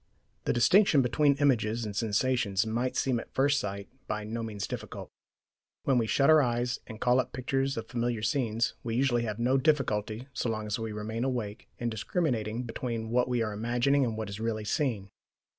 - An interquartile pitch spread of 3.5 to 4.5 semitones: No, average, 3.0 semitones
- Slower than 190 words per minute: No, average, 195 wpm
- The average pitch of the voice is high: No, low, 120 Hz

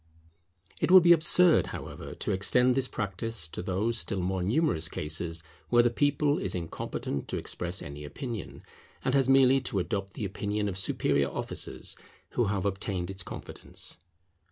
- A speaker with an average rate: Yes, average, 160 wpm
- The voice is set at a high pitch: No, low, 100 Hz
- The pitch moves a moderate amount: No, wide, 6.0 semitones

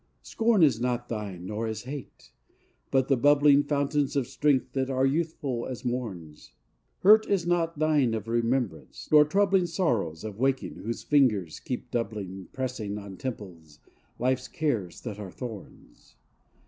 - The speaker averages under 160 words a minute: Yes, average, 150 wpm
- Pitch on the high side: No, low, 125 Hz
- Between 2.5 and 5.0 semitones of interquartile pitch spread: No, wide, 5.4 semitones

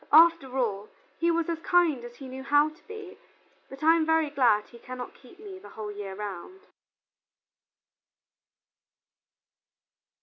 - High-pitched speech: Yes, very high, 285 Hz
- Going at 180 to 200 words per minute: No, average, 145 wpm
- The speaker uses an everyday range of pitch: No, wide, 5.7 semitones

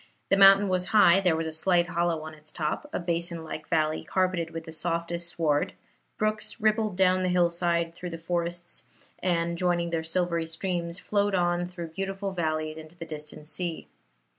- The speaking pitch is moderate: Yes, medium, 170 Hz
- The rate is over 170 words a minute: Yes, average, 180 wpm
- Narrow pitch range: Yes, narrow, 2.0 semitones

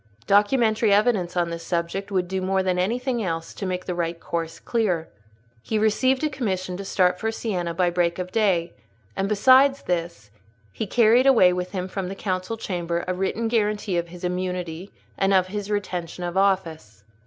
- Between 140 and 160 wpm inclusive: No, average, 185 wpm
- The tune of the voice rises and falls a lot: No, average, 3.2 semitones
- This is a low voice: No, medium, 185 Hz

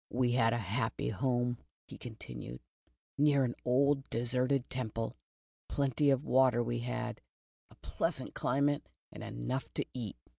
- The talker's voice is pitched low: Yes, low, 125 Hz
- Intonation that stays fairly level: Yes, narrow, 2.2 semitones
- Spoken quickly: No, average, 140 wpm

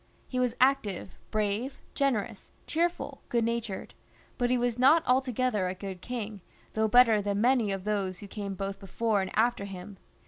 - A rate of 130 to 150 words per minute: No, average, 170 wpm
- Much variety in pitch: No, average, 3.9 semitones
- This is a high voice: Yes, high, 220 Hz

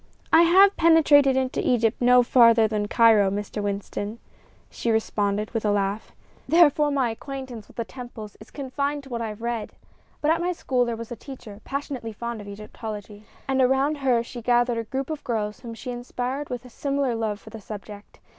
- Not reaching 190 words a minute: No, average, 195 wpm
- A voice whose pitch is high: Yes, high, 240 Hz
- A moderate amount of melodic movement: Yes, average, 3.8 semitones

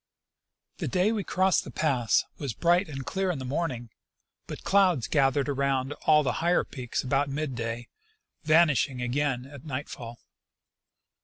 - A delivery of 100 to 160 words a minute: Yes, average, 155 wpm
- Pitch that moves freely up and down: No, average, 4.3 semitones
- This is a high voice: No, medium, 140 Hz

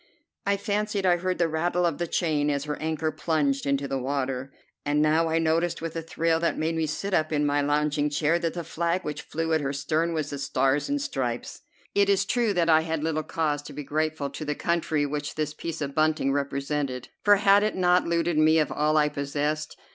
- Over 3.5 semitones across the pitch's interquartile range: No, narrow, 2.5 semitones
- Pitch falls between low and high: Yes, medium, 155 Hz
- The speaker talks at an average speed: No, fast, 225 wpm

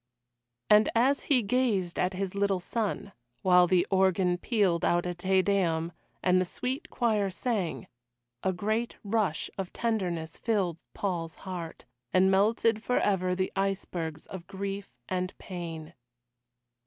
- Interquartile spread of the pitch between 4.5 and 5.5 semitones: No, average, 2.8 semitones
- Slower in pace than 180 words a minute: Yes, slow, 135 wpm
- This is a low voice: No, high, 190 Hz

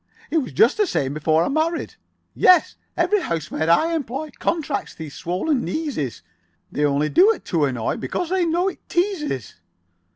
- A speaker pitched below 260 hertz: No, very high, 285 Hz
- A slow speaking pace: No, average, 165 wpm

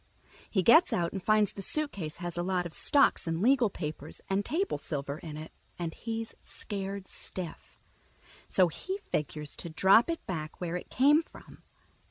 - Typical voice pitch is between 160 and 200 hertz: Yes, medium, 185 Hz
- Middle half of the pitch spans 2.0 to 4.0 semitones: No, wide, 5.6 semitones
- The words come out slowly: No, average, 175 wpm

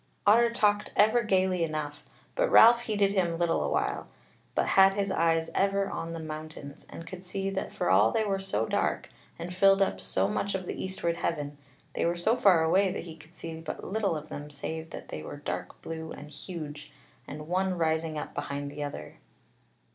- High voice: No, medium, 170 Hz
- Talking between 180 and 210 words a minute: Yes, average, 200 wpm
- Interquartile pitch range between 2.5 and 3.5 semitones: No, average, 4.0 semitones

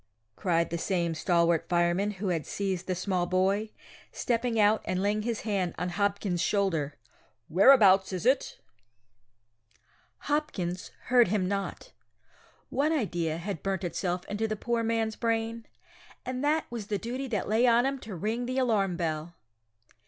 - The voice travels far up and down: No, average, 4.4 semitones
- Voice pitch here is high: Yes, high, 200 Hz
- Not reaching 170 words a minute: Yes, average, 150 wpm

